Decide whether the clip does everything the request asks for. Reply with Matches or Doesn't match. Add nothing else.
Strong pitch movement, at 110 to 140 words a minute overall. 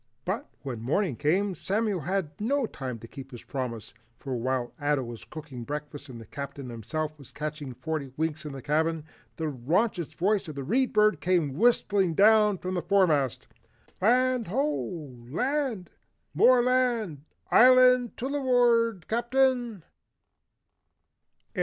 Matches